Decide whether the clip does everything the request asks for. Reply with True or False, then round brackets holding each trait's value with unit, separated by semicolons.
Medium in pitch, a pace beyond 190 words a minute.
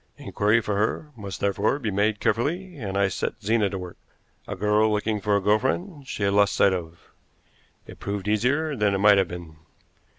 False (105 Hz; 200 wpm)